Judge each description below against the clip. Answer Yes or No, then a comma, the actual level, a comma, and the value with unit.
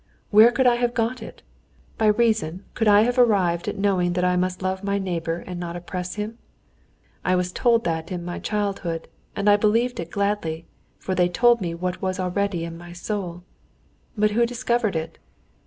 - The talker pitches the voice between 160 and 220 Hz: Yes, high, 190 Hz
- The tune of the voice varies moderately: Yes, average, 3.8 semitones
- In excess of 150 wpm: Yes, average, 190 wpm